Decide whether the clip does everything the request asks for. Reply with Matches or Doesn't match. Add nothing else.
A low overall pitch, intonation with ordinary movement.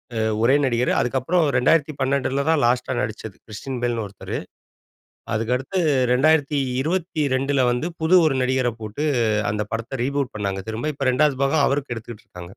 Matches